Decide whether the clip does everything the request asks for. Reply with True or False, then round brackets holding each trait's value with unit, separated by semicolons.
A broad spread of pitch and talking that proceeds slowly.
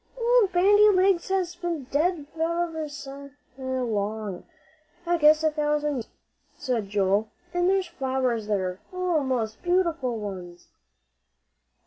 True (7.5 semitones; 125 wpm)